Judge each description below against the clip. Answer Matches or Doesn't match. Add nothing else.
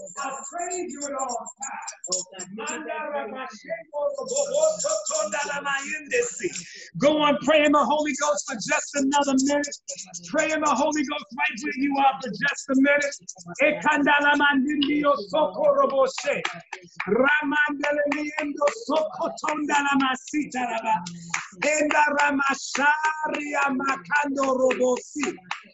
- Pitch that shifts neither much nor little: Doesn't match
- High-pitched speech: Matches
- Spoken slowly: Matches